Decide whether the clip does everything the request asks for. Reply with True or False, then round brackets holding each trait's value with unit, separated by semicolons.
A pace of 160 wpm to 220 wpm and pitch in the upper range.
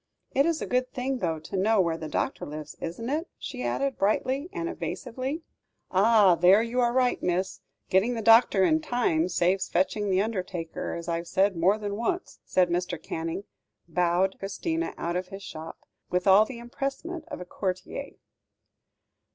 True (175 wpm; 195 Hz)